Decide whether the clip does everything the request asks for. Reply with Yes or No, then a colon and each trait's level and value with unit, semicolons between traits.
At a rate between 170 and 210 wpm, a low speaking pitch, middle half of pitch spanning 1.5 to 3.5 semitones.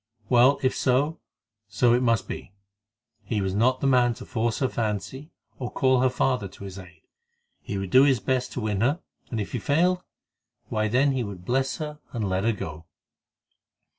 No: average, 195 wpm; low, 120 Hz; average, 4.3 semitones